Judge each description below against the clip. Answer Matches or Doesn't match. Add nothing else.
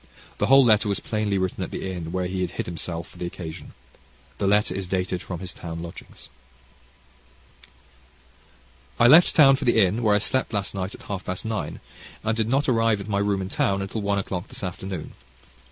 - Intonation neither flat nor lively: Matches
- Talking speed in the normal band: Doesn't match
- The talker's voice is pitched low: Matches